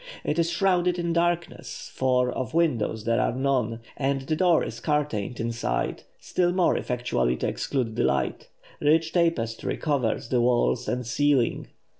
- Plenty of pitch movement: Yes, wide, 6.0 semitones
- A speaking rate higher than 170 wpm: No, average, 155 wpm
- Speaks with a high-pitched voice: No, low, 135 Hz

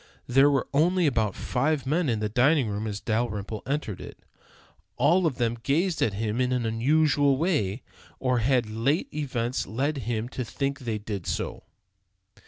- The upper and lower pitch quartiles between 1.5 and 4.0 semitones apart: No, average, 4.5 semitones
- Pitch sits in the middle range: No, low, 125 Hz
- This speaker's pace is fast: No, average, 175 wpm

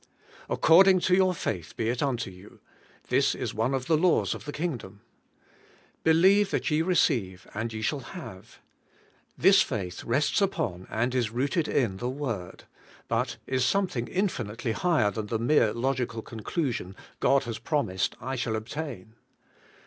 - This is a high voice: No, low, 125 Hz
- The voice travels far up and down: Yes, wide, 6.3 semitones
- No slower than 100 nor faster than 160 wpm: Yes, average, 155 wpm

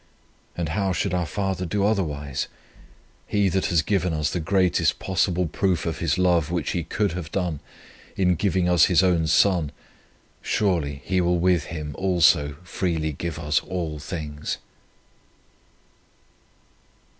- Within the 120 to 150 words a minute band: Yes, average, 145 wpm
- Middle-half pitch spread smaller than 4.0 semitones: Yes, average, 3.0 semitones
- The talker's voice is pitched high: No, very low, 85 Hz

